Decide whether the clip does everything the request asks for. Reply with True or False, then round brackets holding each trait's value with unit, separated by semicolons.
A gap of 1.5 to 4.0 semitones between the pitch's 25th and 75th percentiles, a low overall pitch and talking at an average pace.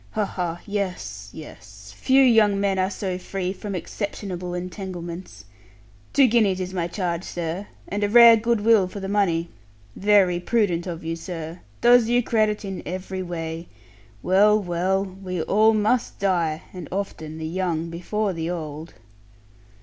False (3.4 semitones; 185 Hz; 155 wpm)